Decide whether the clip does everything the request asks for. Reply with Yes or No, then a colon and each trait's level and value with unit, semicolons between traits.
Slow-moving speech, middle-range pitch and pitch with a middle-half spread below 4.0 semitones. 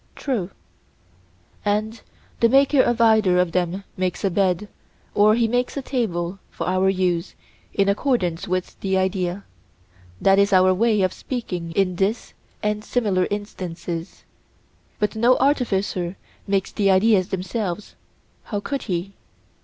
No: slow, 130 wpm; high, 195 Hz; average, 3.3 semitones